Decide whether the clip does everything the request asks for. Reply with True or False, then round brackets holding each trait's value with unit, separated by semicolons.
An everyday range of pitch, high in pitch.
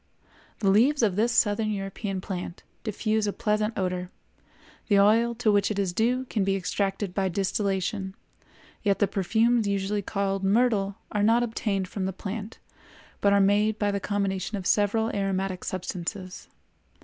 False (2.0 semitones; 200 Hz)